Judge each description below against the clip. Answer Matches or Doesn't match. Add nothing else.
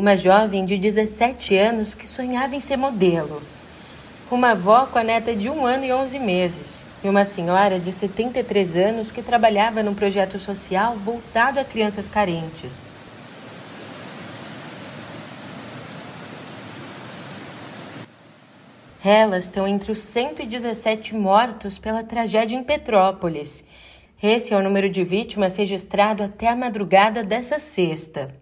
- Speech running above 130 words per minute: Doesn't match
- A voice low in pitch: Doesn't match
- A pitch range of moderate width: Matches